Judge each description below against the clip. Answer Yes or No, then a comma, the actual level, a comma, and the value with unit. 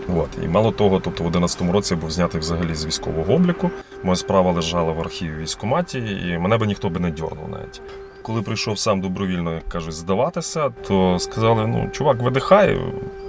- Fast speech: Yes, fast, 185 wpm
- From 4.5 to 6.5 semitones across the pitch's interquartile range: Yes, average, 4.8 semitones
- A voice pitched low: Yes, very low, 95 Hz